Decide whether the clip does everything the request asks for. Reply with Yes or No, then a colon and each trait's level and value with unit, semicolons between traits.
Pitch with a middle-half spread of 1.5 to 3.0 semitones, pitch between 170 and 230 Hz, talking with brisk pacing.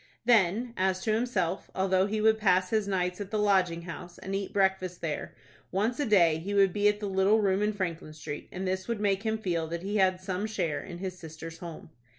Yes: average, 2.7 semitones; high, 190 Hz; fast, 225 wpm